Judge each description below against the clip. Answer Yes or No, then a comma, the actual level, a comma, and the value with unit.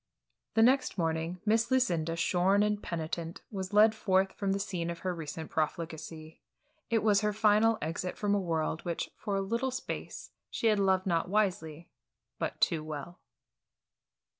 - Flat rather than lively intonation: No, average, 4.2 semitones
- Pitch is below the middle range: No, medium, 185 Hz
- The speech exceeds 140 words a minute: Yes, average, 165 wpm